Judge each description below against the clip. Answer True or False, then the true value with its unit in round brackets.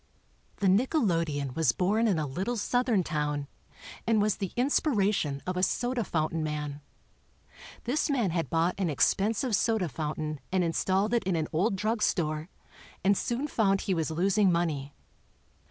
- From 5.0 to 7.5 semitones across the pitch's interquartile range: True (5.6 semitones)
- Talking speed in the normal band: True (155 wpm)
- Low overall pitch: False (185 Hz)